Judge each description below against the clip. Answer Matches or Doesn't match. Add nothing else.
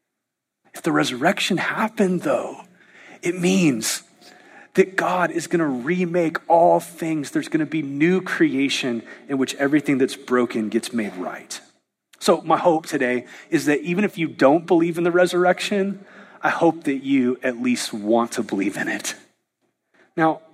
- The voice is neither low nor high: Matches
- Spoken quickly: Doesn't match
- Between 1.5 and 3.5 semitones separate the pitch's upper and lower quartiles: Doesn't match